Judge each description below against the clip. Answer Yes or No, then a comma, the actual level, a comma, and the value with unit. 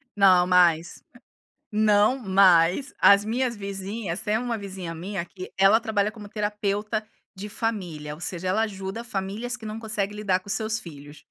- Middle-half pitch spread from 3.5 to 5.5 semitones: No, average, 2.8 semitones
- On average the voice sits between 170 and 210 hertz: Yes, high, 200 Hz